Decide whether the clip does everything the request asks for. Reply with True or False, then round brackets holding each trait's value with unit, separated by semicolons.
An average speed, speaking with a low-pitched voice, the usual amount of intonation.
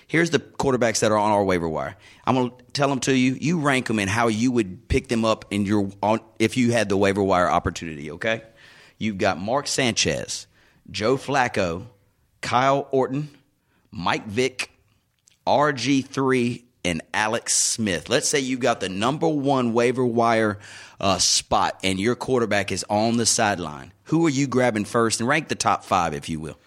True (180 wpm; 115 Hz; 4.4 semitones)